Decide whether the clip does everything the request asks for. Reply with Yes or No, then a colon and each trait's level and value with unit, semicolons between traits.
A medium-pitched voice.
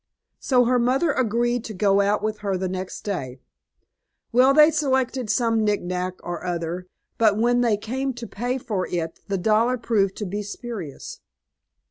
No: high, 215 Hz